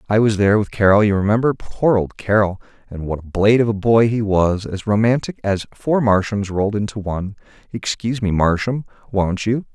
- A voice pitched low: Yes, low, 105 Hz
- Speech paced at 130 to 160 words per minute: No, average, 185 wpm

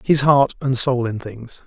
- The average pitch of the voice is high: No, low, 130 Hz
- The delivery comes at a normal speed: No, fast, 215 wpm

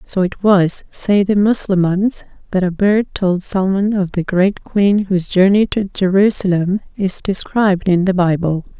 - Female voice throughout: Yes, female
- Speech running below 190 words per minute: Yes, average, 165 wpm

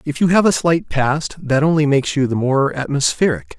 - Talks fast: Yes, fast, 215 wpm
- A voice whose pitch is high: No, medium, 145 Hz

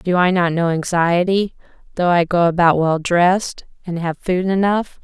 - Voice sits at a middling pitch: Yes, medium, 175 Hz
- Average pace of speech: Yes, average, 180 wpm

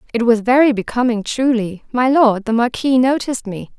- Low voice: No, high, 240 Hz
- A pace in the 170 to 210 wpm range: No, average, 160 wpm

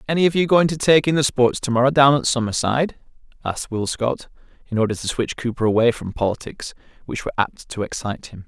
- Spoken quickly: Yes, fast, 210 wpm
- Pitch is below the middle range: Yes, low, 130 Hz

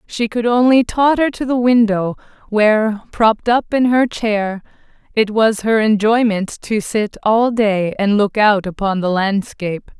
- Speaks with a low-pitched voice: No, high, 220 Hz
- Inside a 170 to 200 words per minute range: No, average, 160 wpm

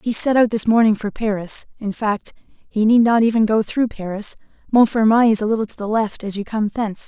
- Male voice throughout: No, female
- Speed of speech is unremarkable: No, fast, 230 wpm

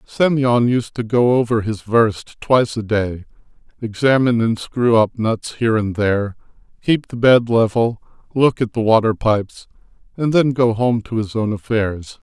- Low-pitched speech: Yes, low, 115 Hz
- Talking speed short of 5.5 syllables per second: Yes, 4.6 syllables/s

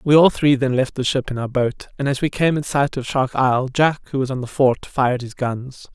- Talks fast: Yes, fast, 280 wpm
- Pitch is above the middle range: No, low, 135 Hz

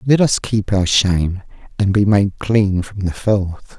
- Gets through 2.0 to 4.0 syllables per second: Yes, 3.9 syllables/s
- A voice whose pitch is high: No, low, 100 Hz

